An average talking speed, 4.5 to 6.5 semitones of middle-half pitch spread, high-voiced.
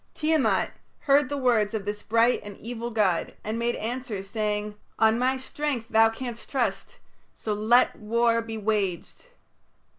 No: average, 150 wpm; average, 2.8 semitones; high, 225 Hz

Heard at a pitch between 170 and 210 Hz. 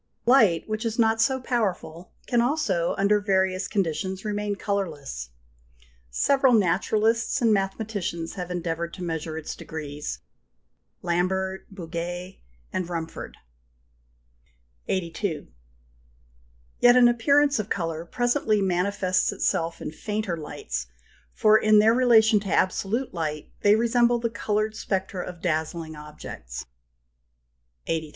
Yes: high, 190 Hz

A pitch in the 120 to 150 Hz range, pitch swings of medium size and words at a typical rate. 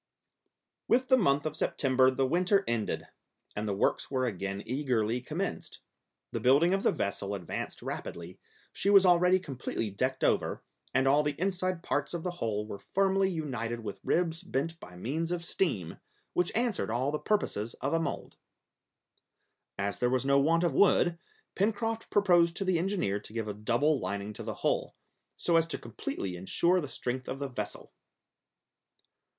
No: medium, 140 Hz; wide, 7.8 semitones; average, 170 wpm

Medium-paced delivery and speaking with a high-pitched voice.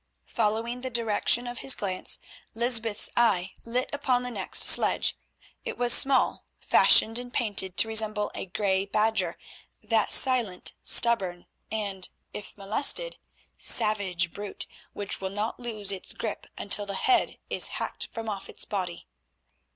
Yes: average, 145 wpm; high, 215 Hz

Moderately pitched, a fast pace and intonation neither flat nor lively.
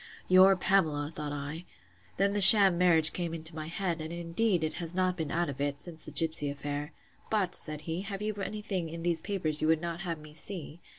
Yes: medium, 165 Hz; fast, 220 wpm; average, 3.2 semitones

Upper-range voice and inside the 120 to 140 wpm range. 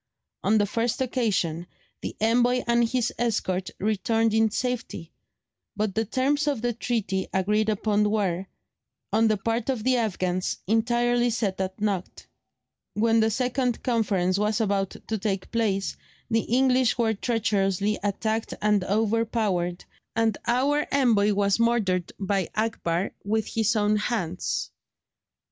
Yes: high, 220 Hz; slow, 135 wpm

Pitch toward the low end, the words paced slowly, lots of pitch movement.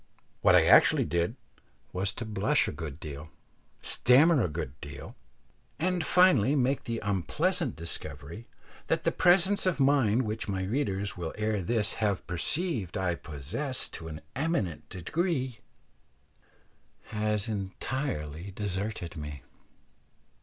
Yes: low, 105 Hz; slow, 125 wpm; wide, 7.8 semitones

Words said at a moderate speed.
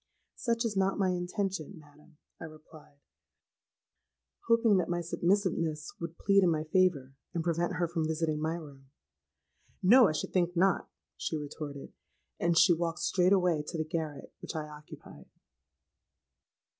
Yes: average, 145 wpm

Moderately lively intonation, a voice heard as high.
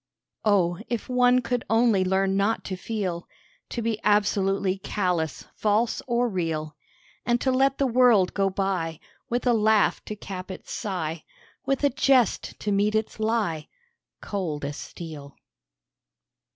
Yes: average, 4.3 semitones; high, 205 Hz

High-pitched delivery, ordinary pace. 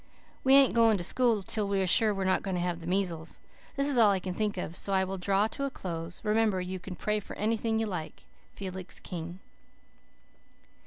No: high, 195 Hz; fast, 220 wpm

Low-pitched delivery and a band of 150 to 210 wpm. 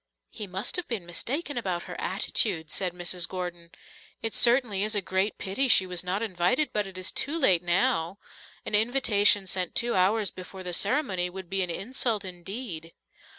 No: high, 190 Hz; average, 180 wpm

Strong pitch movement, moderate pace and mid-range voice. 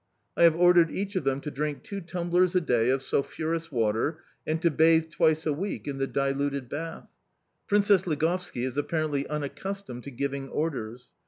No: average, 3.8 semitones; average, 175 wpm; medium, 155 Hz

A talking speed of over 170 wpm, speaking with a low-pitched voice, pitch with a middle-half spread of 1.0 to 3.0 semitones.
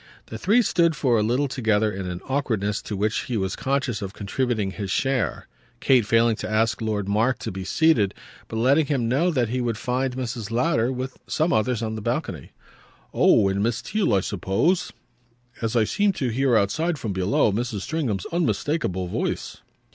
No: average, 185 wpm; low, 115 Hz; average, 4.5 semitones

